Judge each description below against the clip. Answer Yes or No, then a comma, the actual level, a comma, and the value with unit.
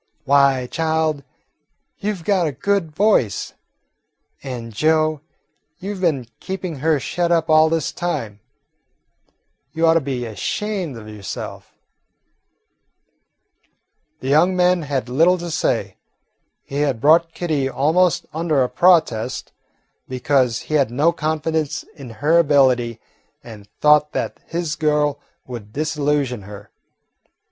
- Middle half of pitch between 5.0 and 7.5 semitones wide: No, average, 4.3 semitones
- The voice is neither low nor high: Yes, medium, 150 Hz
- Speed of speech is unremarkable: No, slow, 125 wpm